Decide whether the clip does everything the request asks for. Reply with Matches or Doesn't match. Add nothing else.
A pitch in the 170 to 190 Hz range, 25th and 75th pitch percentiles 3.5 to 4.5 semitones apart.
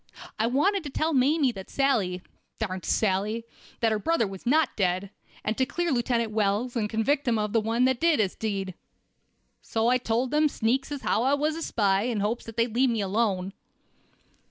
Doesn't match